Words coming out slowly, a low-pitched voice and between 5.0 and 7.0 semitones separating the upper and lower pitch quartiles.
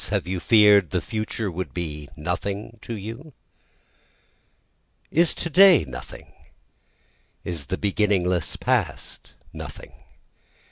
No: slow, 105 wpm; low, 100 Hz; average, 4.3 semitones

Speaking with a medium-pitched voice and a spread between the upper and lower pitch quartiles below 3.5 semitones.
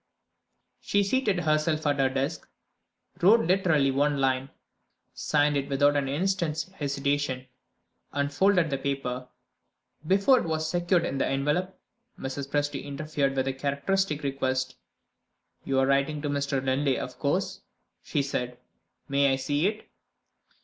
Yes: medium, 145 Hz; average, 2.9 semitones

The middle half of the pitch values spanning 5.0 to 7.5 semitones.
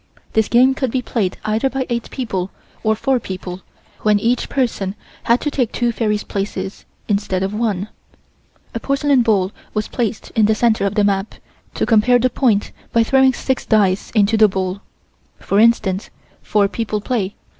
No: average, 3.4 semitones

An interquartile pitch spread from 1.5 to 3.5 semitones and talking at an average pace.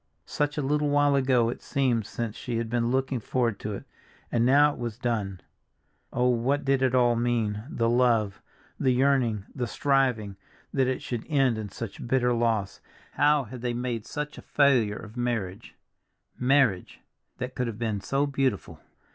Yes: average, 2.9 semitones; average, 170 wpm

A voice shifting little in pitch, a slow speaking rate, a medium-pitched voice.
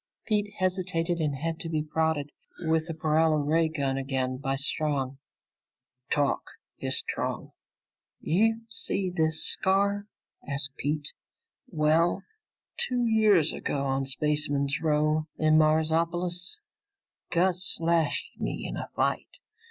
No: average, 3.1 semitones; slow, 120 wpm; medium, 160 Hz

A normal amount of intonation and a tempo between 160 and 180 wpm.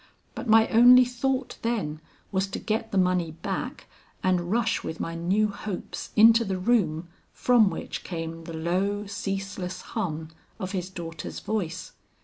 No: average, 4.5 semitones; average, 150 wpm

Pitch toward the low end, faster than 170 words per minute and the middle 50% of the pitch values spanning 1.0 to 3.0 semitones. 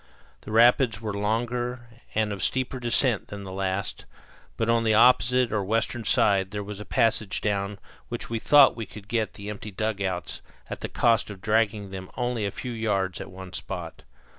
Yes: low, 110 Hz; average, 190 wpm; average, 2.7 semitones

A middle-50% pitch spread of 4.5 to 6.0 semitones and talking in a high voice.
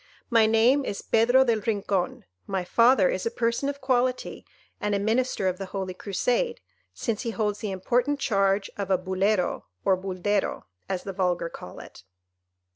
No: average, 4.0 semitones; high, 210 Hz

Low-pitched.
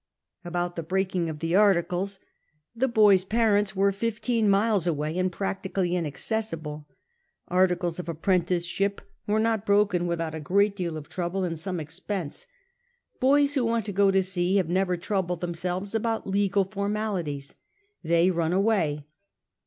No: medium, 185 Hz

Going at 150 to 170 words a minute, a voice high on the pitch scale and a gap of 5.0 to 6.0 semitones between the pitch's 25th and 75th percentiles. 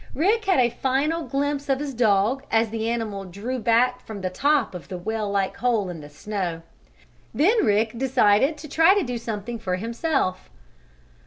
No: average, 180 wpm; high, 230 Hz; average, 5.3 semitones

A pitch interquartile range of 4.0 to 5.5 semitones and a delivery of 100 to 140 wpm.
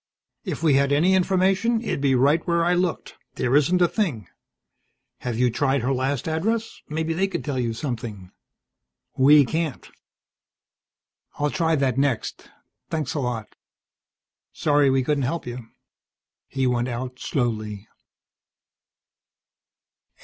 Yes: average, 4.8 semitones; slow, 135 wpm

